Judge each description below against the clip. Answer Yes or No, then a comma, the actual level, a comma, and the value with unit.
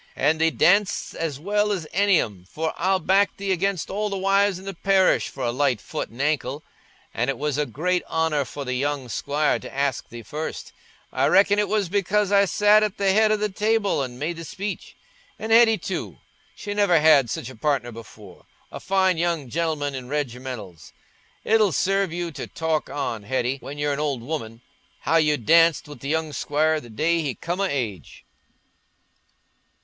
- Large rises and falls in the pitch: Yes, wide, 6.1 semitones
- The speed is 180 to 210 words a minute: Yes, average, 190 wpm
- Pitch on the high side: No, medium, 160 Hz